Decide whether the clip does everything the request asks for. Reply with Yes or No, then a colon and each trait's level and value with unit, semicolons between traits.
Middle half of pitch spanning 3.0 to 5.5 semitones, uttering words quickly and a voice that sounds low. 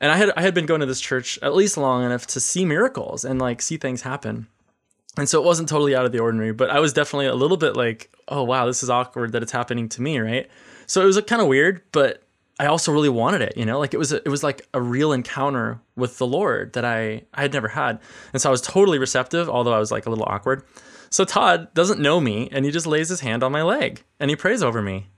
Yes: average, 3.6 semitones; fast, 275 wpm; low, 130 Hz